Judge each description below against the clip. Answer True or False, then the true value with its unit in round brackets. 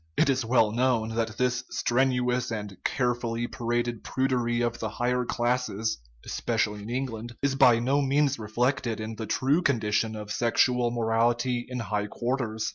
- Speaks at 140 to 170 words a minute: True (155 wpm)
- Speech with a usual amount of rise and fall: False (2.1 semitones)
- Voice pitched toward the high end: False (120 Hz)